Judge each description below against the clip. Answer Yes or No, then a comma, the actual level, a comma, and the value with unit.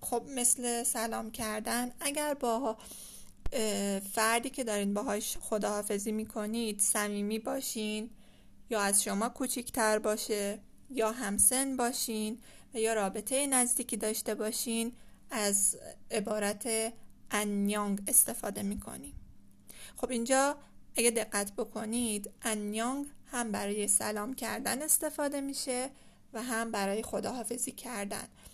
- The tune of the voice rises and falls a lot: No, average, 2.7 semitones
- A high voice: Yes, high, 225 Hz